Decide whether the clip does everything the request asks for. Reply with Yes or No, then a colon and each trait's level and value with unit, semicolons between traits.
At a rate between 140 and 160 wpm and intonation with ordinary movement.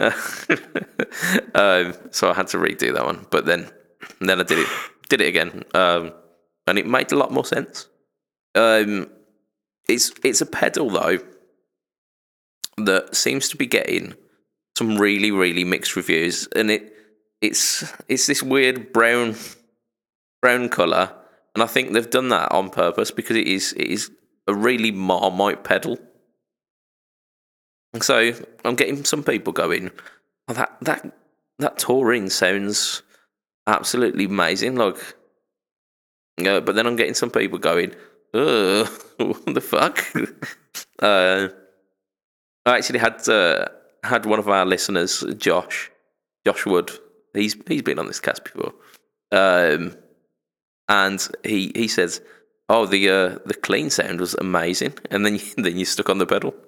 Yes: average, 145 wpm; average, 3.9 semitones